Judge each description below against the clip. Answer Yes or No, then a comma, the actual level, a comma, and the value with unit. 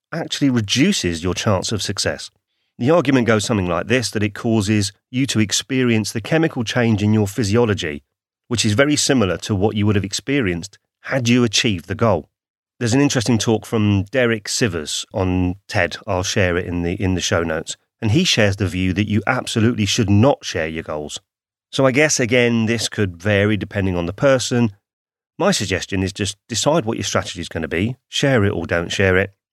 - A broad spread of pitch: No, average, 3.8 semitones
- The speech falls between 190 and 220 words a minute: Yes, average, 200 wpm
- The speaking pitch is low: Yes, low, 105 Hz